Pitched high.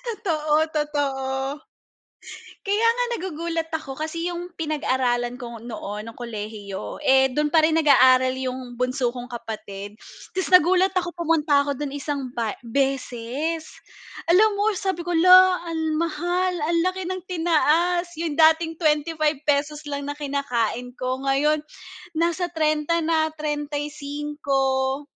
Yes: very high, 300 Hz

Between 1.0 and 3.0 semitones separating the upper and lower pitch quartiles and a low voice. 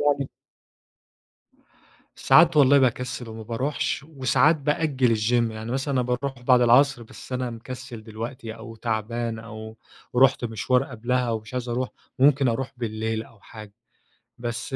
Yes: average, 2.7 semitones; low, 120 Hz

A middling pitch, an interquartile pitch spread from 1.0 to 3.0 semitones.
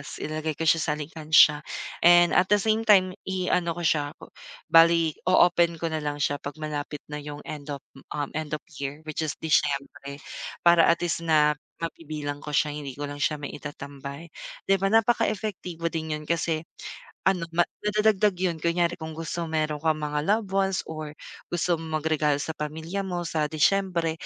Yes: medium, 160 Hz; narrow, 2.6 semitones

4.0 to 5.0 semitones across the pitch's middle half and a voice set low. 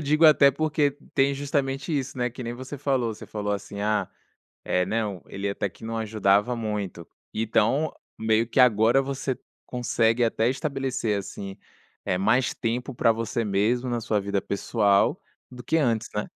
Yes: average, 4.3 semitones; low, 115 Hz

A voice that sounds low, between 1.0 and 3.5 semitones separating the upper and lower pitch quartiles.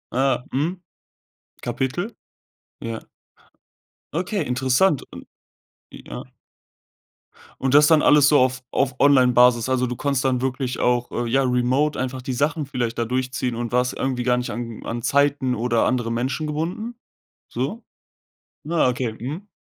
Yes: low, 130 Hz; narrow, 2.6 semitones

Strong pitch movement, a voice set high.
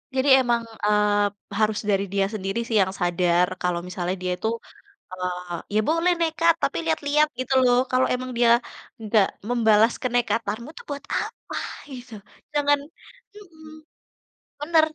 Yes: wide, 6.3 semitones; high, 230 Hz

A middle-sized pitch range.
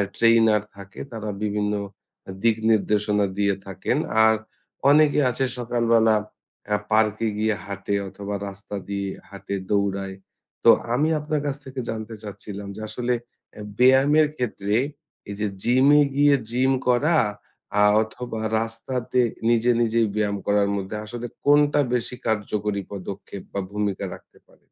Yes: average, 3.3 semitones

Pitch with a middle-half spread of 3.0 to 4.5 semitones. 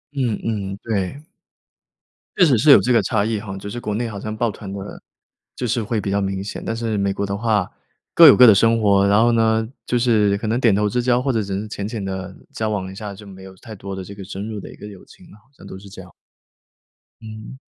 No: narrow, 2.5 semitones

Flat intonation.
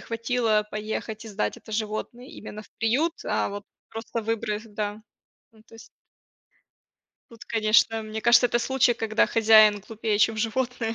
Yes: narrow, 1.4 semitones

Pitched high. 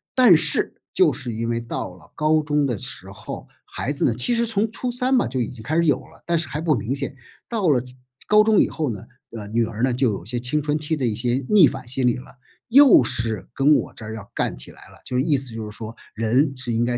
No: low, 130 Hz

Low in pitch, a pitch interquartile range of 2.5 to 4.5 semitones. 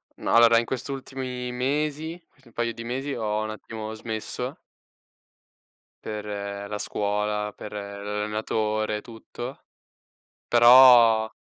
Yes: low, 115 Hz; average, 2.8 semitones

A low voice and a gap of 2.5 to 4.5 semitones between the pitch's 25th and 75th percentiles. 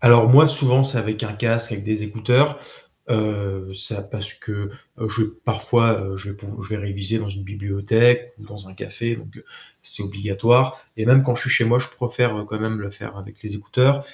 Yes: low, 110 Hz; average, 3.1 semitones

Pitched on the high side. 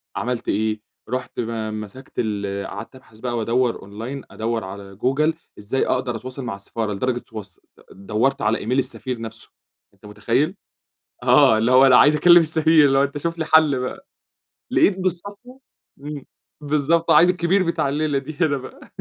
No: low, 130 Hz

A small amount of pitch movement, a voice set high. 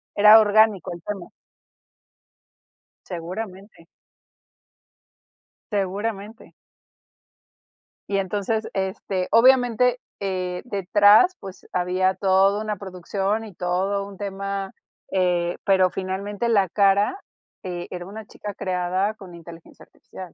Yes: narrow, 2.1 semitones; high, 195 Hz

